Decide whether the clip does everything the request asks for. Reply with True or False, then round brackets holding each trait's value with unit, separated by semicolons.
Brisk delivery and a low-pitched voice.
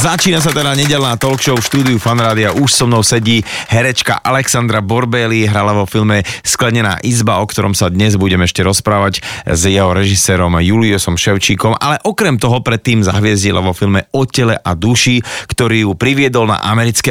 True (170 wpm; 115 Hz)